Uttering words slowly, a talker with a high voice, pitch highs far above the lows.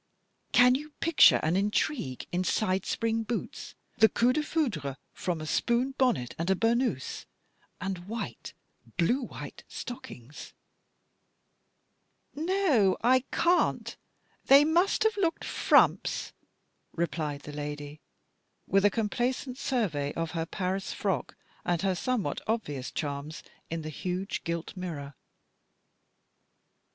Yes: slow, 120 wpm; high, 195 Hz; wide, 7.8 semitones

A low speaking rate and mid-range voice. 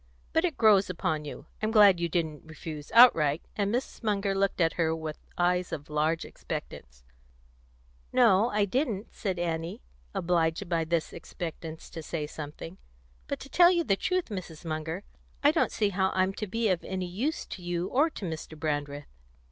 No: average, 180 wpm; medium, 180 Hz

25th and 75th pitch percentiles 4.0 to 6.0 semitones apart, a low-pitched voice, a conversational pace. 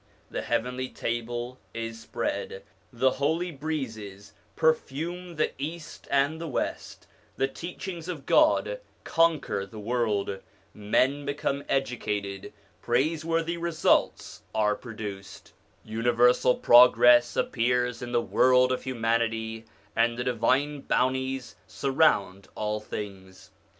No: average, 4.6 semitones; low, 125 Hz; slow, 110 wpm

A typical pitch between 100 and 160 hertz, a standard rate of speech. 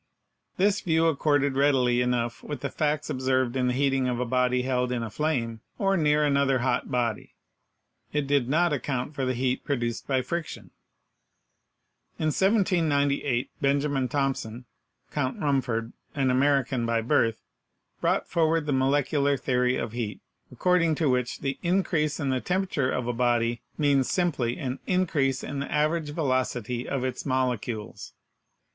Yes: low, 135 Hz; average, 160 wpm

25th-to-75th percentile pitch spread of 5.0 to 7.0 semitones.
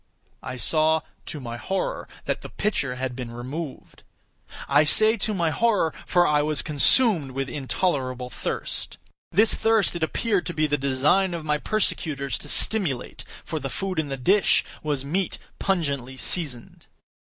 Yes: wide, 5.4 semitones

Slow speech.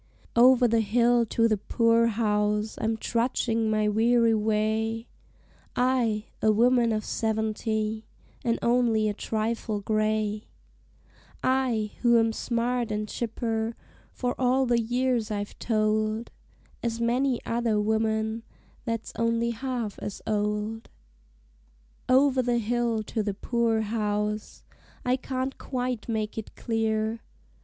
Yes: slow, 120 wpm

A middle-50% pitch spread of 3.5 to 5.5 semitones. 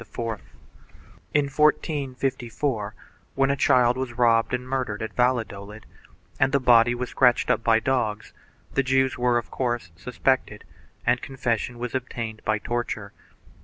No: narrow, 2.5 semitones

